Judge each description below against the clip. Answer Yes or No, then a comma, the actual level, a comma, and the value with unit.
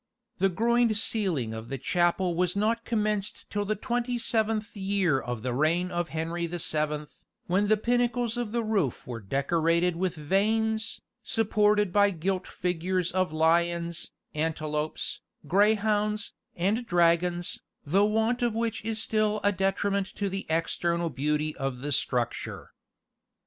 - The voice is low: No, medium, 185 Hz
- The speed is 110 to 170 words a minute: Yes, average, 145 wpm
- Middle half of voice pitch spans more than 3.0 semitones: Yes, average, 4.7 semitones